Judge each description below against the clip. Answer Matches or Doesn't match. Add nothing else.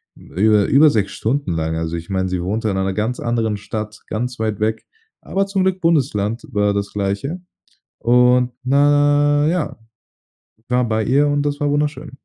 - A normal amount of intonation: Doesn't match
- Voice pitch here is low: Matches